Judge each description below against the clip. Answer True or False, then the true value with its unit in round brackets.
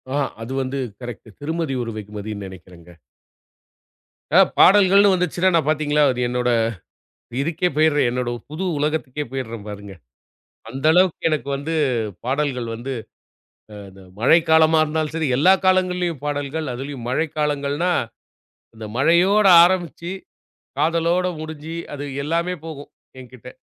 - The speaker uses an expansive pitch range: False (4.6 semitones)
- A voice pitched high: False (150 Hz)